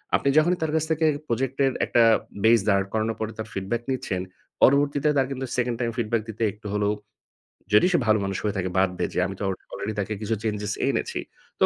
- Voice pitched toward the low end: Yes, low, 110 Hz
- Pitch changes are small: No, average, 4.2 semitones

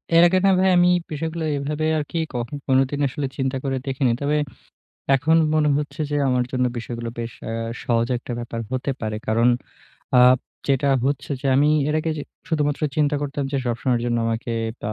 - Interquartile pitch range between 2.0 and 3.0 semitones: No, average, 3.5 semitones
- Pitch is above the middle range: No, medium, 140 Hz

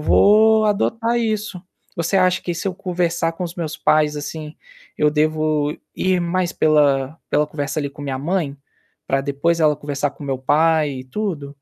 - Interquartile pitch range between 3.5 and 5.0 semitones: Yes, average, 3.9 semitones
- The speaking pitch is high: No, medium, 155 Hz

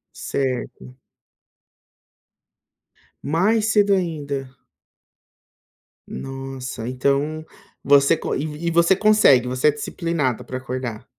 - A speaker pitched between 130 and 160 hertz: Yes, medium, 140 Hz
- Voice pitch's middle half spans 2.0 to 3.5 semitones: No, average, 4.5 semitones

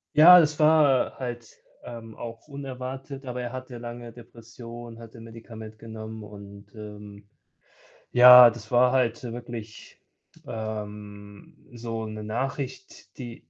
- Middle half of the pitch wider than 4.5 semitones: No, narrow, 2.5 semitones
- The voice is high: No, low, 115 Hz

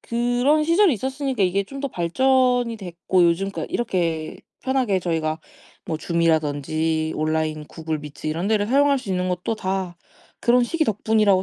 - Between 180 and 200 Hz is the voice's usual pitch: Yes, high, 190 Hz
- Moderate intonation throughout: No, wide, 7.2 semitones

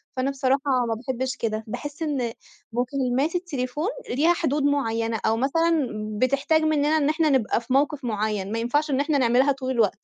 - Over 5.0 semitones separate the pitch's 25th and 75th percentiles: No, average, 3.5 semitones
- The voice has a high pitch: Yes, very high, 265 Hz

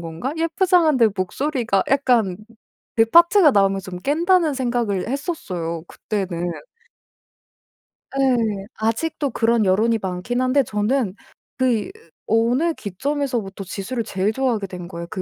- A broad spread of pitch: Yes, wide, 6.0 semitones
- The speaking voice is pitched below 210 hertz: No, high, 230 Hz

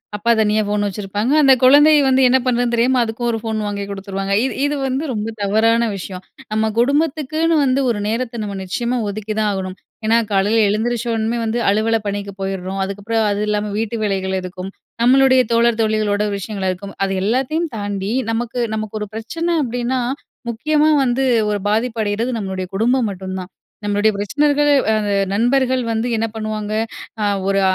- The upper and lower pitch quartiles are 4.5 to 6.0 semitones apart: No, average, 3.4 semitones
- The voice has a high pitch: Yes, high, 220 Hz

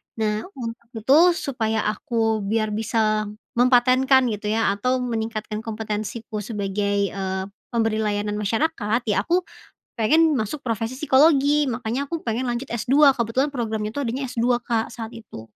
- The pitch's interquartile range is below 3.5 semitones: Yes, average, 3.1 semitones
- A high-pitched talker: Yes, high, 225 Hz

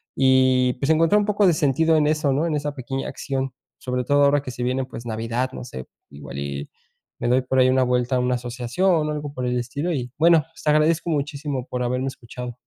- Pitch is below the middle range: Yes, low, 130 Hz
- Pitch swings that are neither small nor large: Yes, average, 3.3 semitones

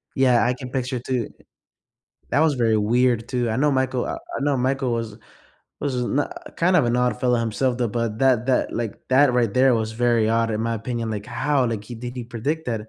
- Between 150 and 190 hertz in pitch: No, low, 125 Hz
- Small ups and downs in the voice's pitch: Yes, narrow, 2.3 semitones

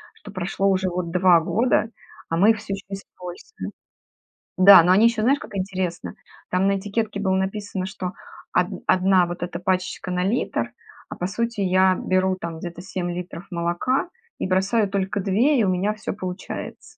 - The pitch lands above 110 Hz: Yes, high, 190 Hz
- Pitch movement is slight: Yes, narrow, 2.1 semitones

